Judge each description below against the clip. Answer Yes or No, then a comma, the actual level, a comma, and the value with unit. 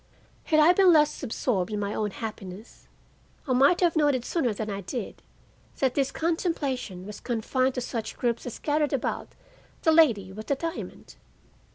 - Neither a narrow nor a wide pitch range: No, wide, 6.0 semitones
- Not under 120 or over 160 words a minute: No, average, 170 wpm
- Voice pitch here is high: Yes, very high, 255 Hz